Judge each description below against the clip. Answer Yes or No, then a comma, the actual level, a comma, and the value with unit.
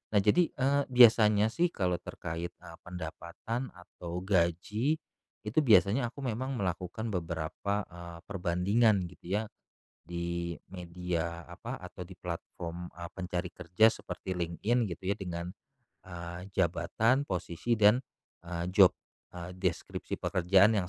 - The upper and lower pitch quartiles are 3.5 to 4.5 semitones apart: Yes, average, 3.8 semitones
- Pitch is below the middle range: Yes, very low, 90 Hz